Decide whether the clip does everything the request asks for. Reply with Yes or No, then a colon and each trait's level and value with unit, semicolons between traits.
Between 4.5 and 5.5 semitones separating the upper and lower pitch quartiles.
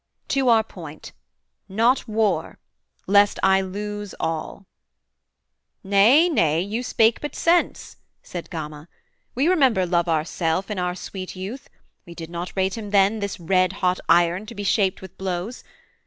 No: average, 3.8 semitones